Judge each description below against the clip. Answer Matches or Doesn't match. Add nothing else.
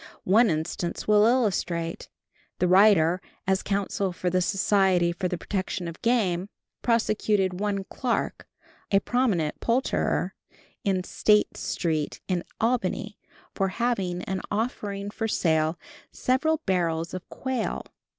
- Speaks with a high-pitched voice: Matches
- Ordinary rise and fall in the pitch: Matches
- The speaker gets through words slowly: Matches